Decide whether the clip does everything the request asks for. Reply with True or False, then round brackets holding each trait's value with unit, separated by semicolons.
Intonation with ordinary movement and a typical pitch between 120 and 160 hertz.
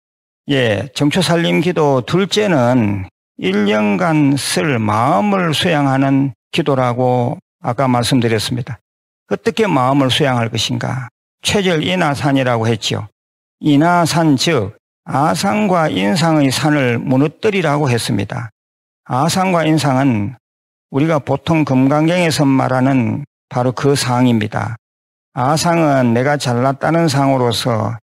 True (4.8 semitones; 135 Hz)